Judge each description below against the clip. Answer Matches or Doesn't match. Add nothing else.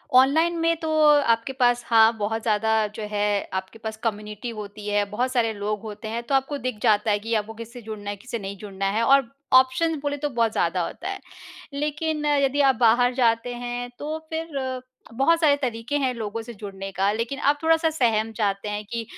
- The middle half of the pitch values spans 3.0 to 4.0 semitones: Doesn't match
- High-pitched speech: Matches